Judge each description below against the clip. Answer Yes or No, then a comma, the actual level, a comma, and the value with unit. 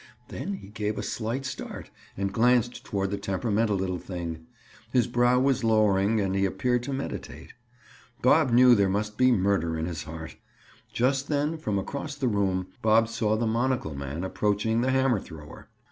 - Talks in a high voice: No, low, 110 Hz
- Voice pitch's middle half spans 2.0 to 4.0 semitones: No, average, 4.5 semitones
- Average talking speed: Yes, average, 175 wpm